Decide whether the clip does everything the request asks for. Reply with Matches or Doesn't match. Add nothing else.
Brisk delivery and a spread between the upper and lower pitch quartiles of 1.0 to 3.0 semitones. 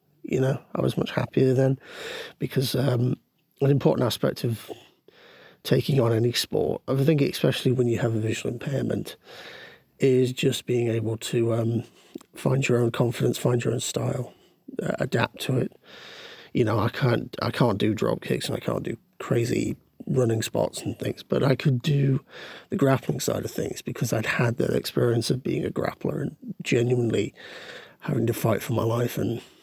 Doesn't match